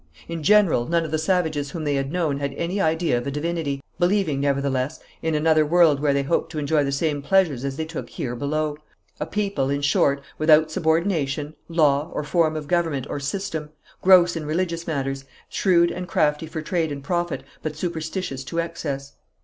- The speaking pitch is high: No, medium, 155 Hz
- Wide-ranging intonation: No, average, 3.1 semitones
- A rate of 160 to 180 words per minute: No, average, 190 wpm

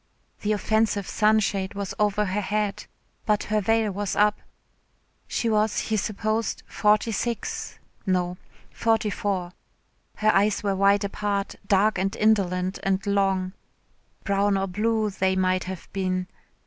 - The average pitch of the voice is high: Yes, high, 200 Hz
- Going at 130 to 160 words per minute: Yes, slow, 135 wpm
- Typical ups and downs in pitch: No, narrow, 1.9 semitones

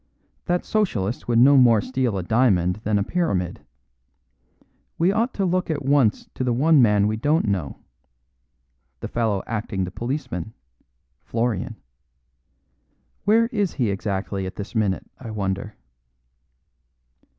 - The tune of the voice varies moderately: No, wide, 6.4 semitones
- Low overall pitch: Yes, low, 115 Hz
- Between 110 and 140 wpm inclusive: Yes, slow, 135 wpm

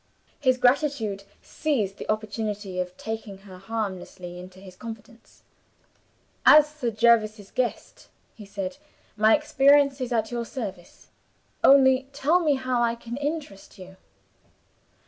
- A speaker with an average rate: No, slow, 125 wpm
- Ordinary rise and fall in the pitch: Yes, average, 5.0 semitones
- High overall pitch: Yes, high, 225 Hz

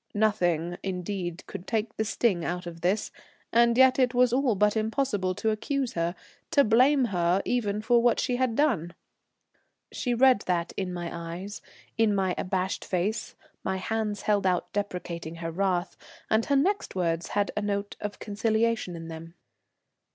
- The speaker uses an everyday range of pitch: Yes, average, 4.5 semitones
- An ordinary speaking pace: Yes, average, 165 wpm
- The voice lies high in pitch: Yes, high, 205 Hz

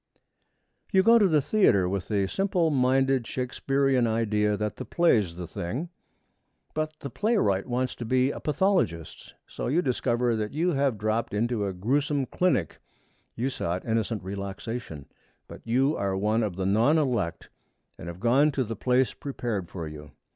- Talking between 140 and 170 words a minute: Yes, average, 165 wpm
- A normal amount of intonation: No, wide, 5.8 semitones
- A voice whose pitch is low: Yes, low, 120 Hz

